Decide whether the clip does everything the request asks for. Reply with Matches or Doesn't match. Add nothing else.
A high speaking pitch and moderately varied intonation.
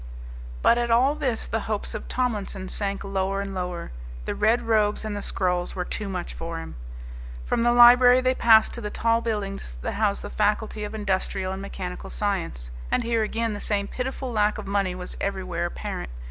Matches